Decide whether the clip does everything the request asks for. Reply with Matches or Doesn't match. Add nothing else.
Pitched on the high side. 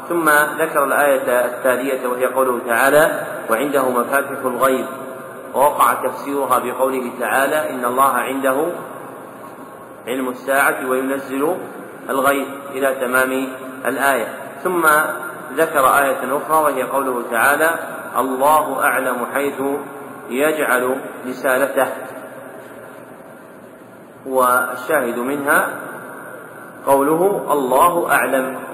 Doesn't match